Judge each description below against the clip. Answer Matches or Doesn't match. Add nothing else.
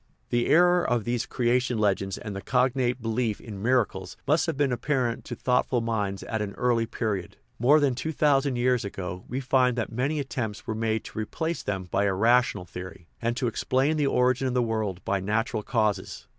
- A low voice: Matches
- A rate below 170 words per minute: Doesn't match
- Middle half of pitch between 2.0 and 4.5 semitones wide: Matches